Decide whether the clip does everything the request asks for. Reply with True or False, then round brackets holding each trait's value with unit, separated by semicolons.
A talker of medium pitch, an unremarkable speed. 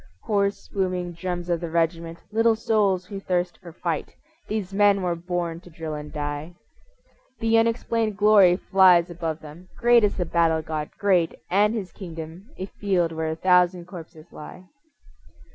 True (180 Hz; 160 wpm)